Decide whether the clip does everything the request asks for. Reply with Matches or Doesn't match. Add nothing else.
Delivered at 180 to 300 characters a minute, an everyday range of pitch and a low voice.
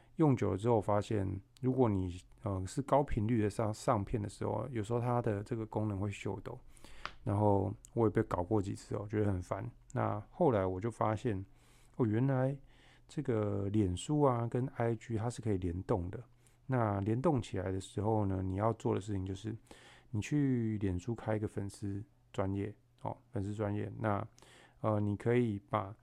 Matches